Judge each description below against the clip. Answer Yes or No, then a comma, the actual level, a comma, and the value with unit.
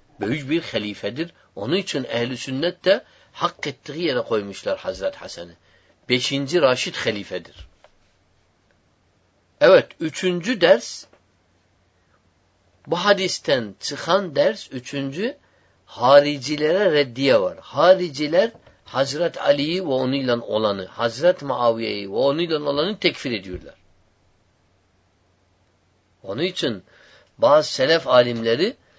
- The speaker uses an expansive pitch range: Yes, wide, 8.8 semitones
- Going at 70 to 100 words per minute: Yes, slow, 95 wpm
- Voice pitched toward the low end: Yes, low, 120 Hz